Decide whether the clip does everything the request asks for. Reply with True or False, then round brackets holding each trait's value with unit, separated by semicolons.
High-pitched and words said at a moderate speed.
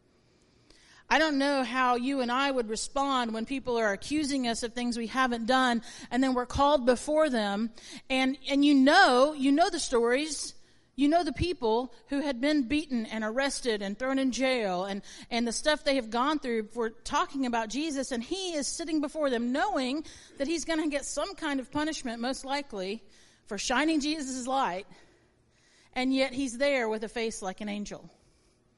True (260 Hz; 190 wpm)